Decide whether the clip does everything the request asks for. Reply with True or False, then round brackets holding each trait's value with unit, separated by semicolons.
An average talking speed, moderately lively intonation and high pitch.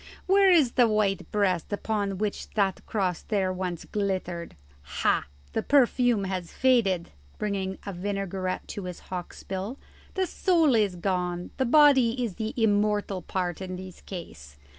True (150 wpm; 3.6 semitones; 195 Hz)